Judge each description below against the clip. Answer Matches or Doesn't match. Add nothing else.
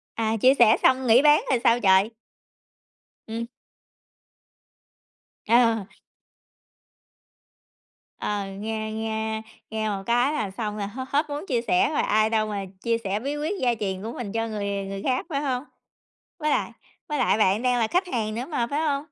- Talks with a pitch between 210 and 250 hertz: Matches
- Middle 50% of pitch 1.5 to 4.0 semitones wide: Matches